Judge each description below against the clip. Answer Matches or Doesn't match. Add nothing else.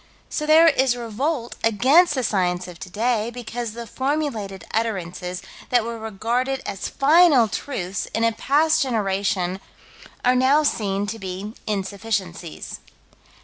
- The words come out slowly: Matches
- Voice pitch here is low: Doesn't match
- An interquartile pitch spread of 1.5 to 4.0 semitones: Doesn't match